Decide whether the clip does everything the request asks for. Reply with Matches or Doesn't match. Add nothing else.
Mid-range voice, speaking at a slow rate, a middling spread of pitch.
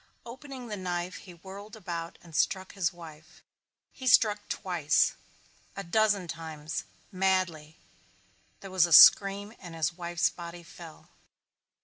Matches